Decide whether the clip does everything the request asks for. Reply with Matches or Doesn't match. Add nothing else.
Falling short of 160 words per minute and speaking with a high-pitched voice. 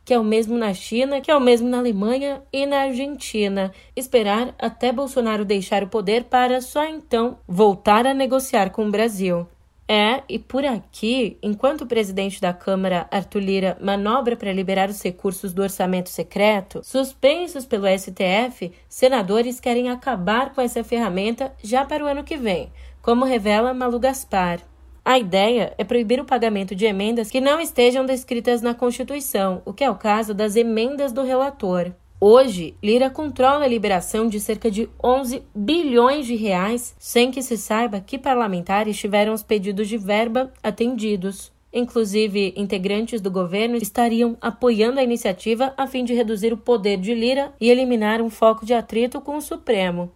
Doesn't match